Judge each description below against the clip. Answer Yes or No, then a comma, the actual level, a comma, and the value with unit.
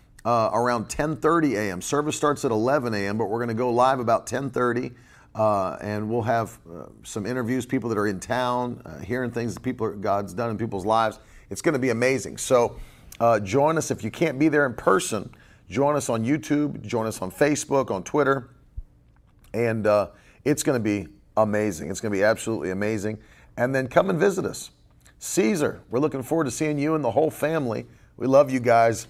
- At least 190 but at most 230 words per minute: Yes, fast, 205 wpm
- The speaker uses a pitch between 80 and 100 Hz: No, low, 120 Hz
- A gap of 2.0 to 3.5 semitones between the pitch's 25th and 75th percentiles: No, average, 4.6 semitones